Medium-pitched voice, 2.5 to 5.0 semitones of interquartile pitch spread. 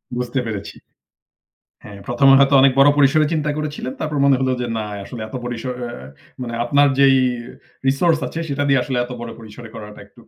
No: low, 130 Hz; average, 2.9 semitones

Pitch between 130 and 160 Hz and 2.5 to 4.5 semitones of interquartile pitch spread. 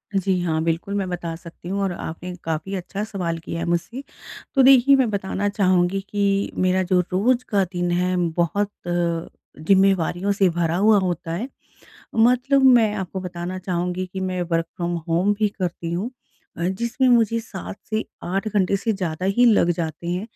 No: medium, 185 Hz; average, 2.9 semitones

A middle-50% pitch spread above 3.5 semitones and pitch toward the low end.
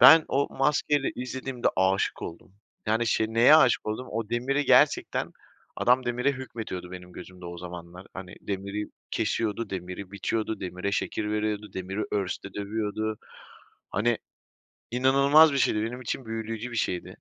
Yes: average, 4.5 semitones; low, 110 Hz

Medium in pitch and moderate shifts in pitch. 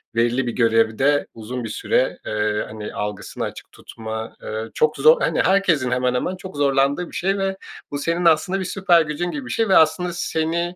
No: medium, 145 Hz; wide, 7.4 semitones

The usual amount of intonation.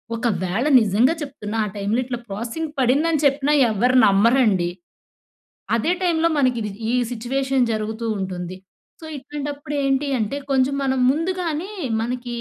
Yes: average, 4.7 semitones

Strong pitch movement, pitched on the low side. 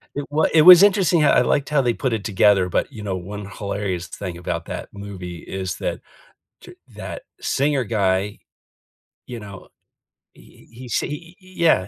Yes: wide, 7.4 semitones; low, 105 Hz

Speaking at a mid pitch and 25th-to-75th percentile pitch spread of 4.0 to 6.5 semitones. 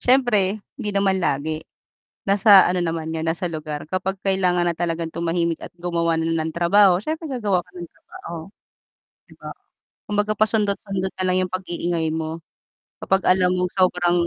No: medium, 180 Hz; average, 2.8 semitones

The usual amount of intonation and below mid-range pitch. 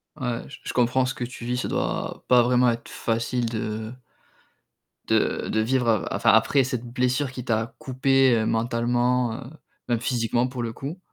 No: narrow, 1.6 semitones; low, 120 Hz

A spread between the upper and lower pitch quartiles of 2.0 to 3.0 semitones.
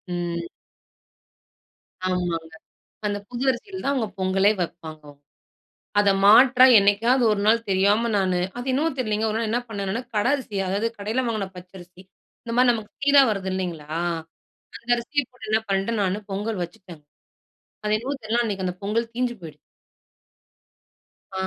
No: average, 4.0 semitones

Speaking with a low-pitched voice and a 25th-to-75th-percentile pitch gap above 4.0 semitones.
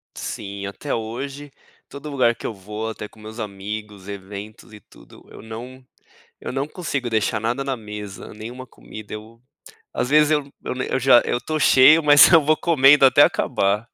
Yes: low, 115 Hz; average, 4.6 semitones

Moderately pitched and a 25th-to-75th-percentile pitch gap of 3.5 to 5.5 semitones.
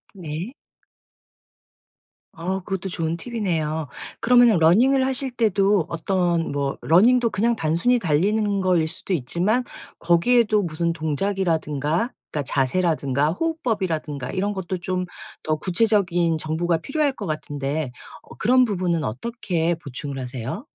Yes: medium, 175 Hz; average, 5.2 semitones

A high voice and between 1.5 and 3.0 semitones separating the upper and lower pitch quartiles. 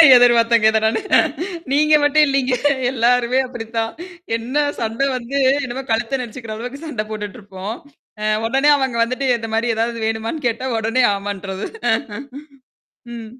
Yes: high, 235 Hz; average, 2.7 semitones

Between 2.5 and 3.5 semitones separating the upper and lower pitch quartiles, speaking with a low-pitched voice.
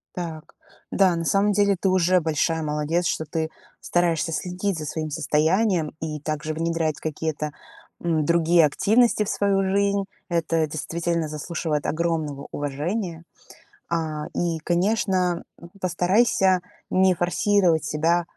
No: average, 2.9 semitones; medium, 170 Hz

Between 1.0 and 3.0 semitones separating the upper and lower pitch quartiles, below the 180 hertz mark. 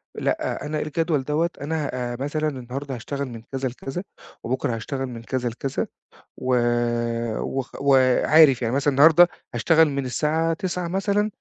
No: average, 3.8 semitones; medium, 140 Hz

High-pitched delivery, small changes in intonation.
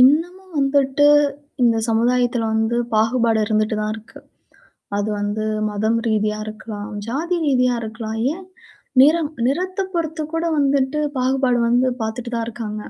No: high, 245 Hz; average, 4.3 semitones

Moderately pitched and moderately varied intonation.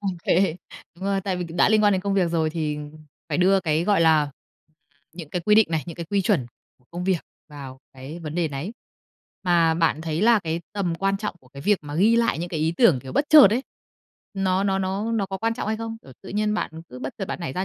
Yes: medium, 180 Hz; average, 4.0 semitones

